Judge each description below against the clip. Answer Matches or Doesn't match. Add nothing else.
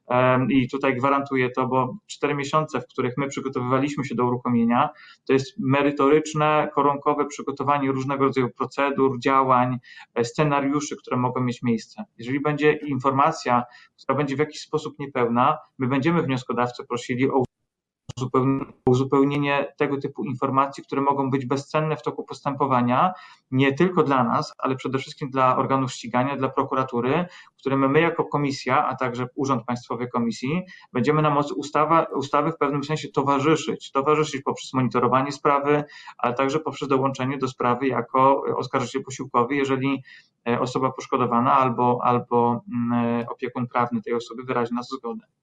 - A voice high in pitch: Doesn't match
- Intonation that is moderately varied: Doesn't match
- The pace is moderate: Matches